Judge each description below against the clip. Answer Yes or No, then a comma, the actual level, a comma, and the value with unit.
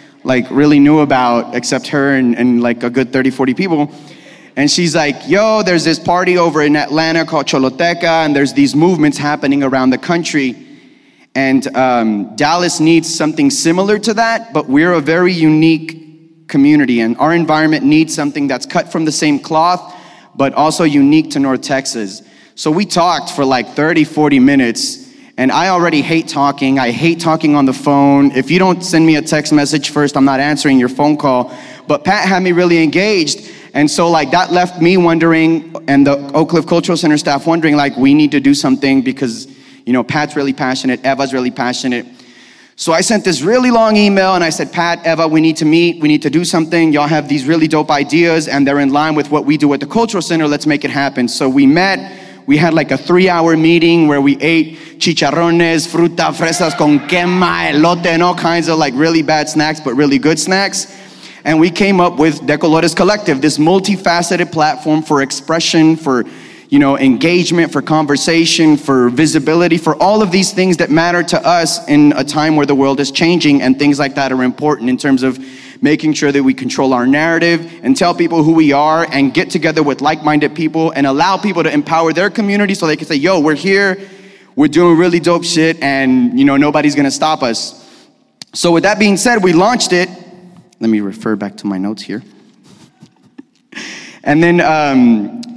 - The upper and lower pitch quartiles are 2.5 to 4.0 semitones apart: Yes, average, 3.4 semitones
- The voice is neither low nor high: Yes, medium, 155 Hz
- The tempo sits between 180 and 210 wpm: Yes, average, 200 wpm